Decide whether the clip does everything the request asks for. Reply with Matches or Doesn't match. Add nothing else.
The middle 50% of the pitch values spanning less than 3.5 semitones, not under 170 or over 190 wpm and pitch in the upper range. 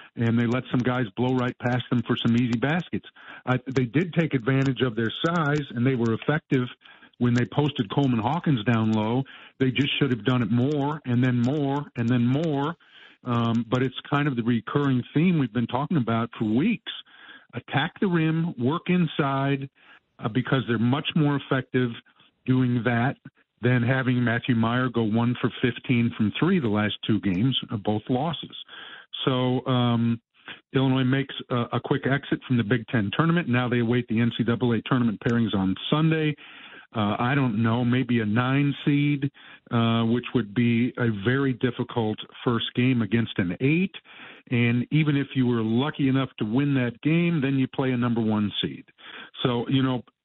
Doesn't match